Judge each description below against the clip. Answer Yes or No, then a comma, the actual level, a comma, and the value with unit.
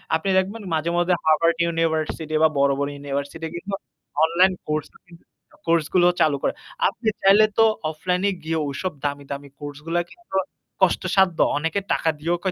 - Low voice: No, medium, 165 Hz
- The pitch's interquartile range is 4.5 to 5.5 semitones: No, average, 3.2 semitones